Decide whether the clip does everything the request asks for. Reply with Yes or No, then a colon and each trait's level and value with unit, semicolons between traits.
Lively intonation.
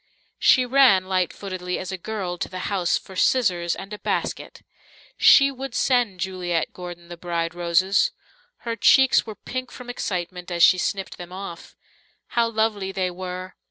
No: average, 3.8 semitones